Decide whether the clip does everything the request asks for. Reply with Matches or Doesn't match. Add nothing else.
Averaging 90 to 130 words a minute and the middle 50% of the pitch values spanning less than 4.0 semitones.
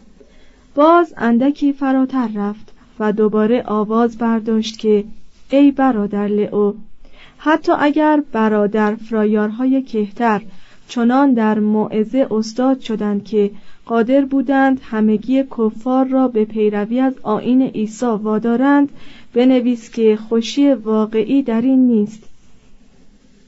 Matches